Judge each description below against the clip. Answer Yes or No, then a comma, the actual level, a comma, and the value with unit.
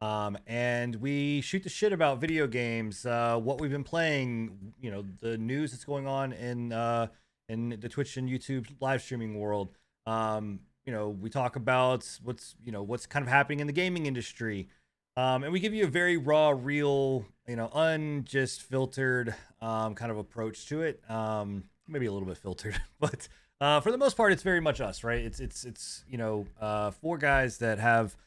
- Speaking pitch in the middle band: No, low, 120 Hz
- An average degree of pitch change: Yes, average, 4.4 semitones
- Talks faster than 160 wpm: Yes, average, 200 wpm